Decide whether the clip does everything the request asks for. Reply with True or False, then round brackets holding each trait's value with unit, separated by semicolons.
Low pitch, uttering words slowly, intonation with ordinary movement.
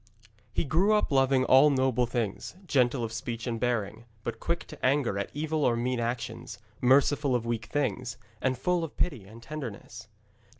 False (125 Hz; 175 wpm; 3.6 semitones)